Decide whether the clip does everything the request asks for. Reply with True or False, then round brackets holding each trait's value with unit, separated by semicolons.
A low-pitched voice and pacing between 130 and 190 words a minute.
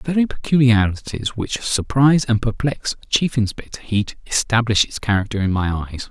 True (115 Hz; 155 wpm)